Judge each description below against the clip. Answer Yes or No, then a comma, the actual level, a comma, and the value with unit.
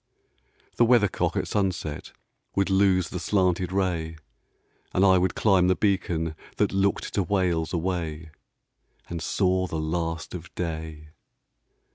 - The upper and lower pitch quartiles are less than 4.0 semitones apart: Yes, average, 2.9 semitones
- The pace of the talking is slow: Yes, slow, 130 wpm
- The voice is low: Yes, very low, 90 Hz